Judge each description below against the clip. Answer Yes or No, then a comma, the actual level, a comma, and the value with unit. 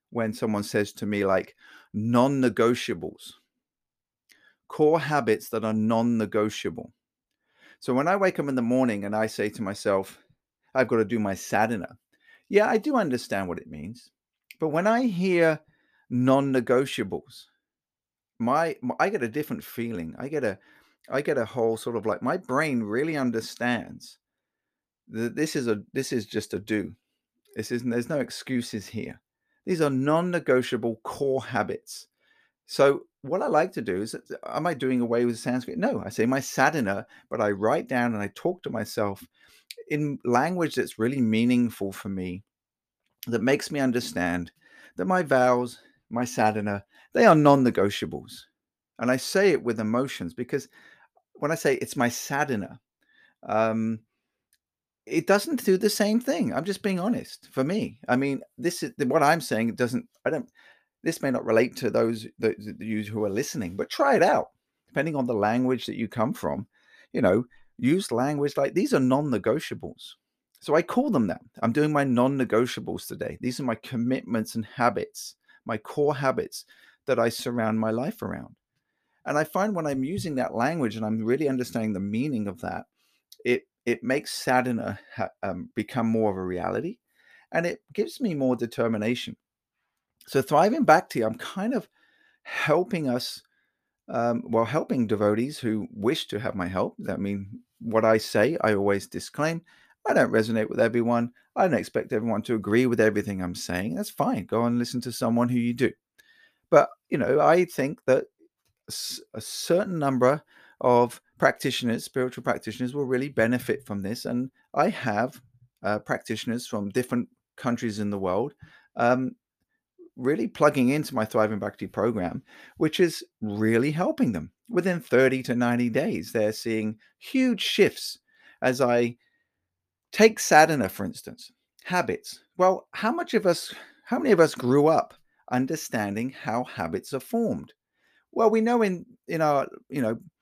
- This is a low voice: Yes, low, 125 Hz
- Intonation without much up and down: No, average, 5.1 semitones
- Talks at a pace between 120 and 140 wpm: No, average, 170 wpm